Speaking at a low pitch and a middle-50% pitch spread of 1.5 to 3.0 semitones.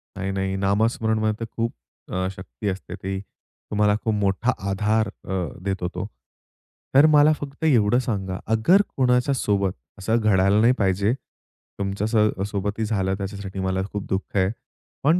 Yes: low, 105 Hz; narrow, 2.6 semitones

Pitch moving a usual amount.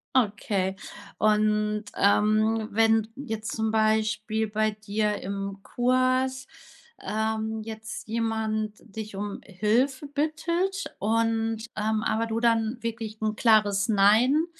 No: narrow, 1.3 semitones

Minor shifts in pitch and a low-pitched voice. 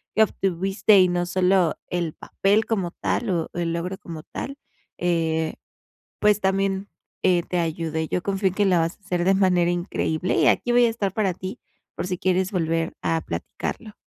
No: narrow, 2.3 semitones; medium, 185 Hz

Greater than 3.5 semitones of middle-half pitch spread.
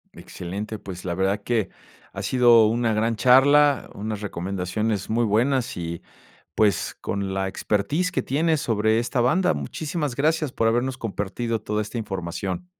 Yes: average, 4.4 semitones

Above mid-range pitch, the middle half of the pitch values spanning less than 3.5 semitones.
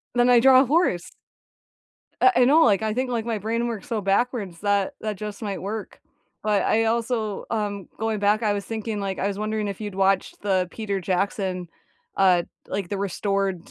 Yes: high, 210 Hz; narrow, 2.4 semitones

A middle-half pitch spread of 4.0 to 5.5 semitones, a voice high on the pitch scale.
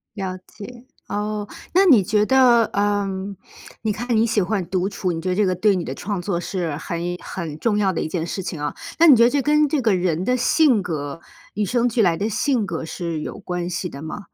Yes: average, 4.7 semitones; high, 200 Hz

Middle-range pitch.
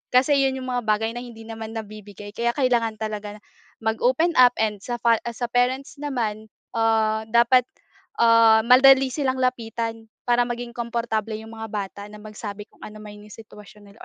No: high, 225 Hz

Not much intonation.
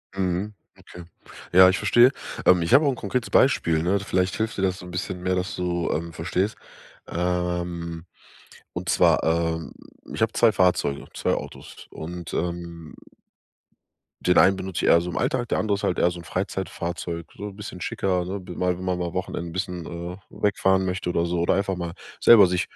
Yes: narrow, 1.8 semitones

